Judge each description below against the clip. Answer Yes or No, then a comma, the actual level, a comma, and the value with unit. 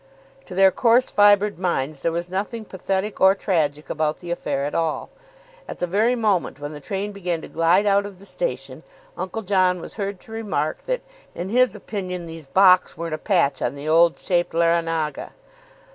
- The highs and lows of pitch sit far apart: No, average, 3.6 semitones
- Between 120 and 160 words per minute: No, average, 190 wpm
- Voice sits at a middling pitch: Yes, medium, 180 Hz